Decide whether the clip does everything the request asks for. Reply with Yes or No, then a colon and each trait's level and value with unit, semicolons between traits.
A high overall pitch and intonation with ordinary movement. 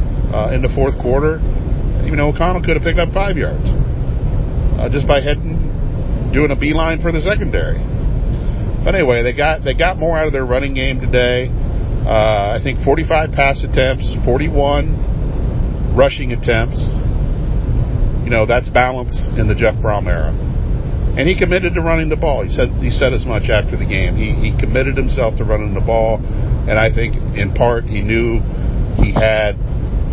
No: low, 125 Hz; average, 4.2 semitones